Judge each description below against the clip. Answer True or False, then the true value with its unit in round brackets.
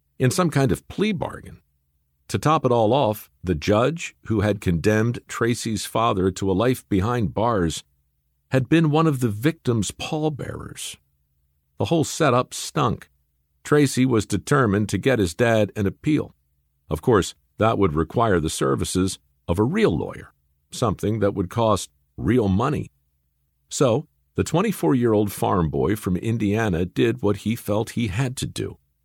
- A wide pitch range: True (6.9 semitones)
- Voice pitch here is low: True (105 Hz)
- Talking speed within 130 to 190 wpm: True (160 wpm)